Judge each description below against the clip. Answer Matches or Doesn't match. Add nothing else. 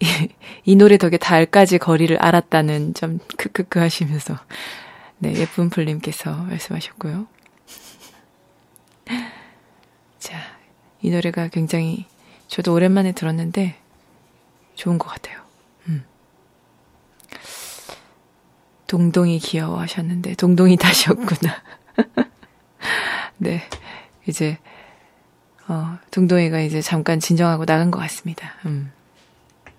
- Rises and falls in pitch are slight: Matches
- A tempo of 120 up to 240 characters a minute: Matches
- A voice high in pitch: Doesn't match